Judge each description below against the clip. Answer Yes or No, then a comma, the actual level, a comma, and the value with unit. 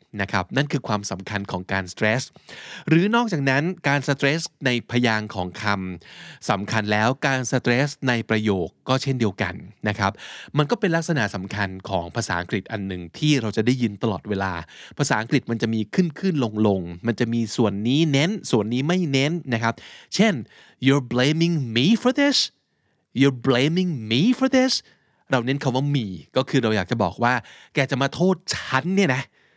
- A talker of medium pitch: No, low, 125 Hz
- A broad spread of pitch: Yes, wide, 5.7 semitones